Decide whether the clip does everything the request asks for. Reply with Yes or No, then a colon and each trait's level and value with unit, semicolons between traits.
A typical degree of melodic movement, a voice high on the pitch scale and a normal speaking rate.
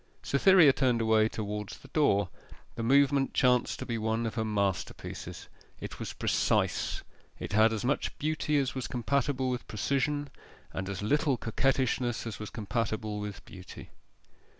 No: average, 4.2 semitones; low, 115 Hz; average, 150 wpm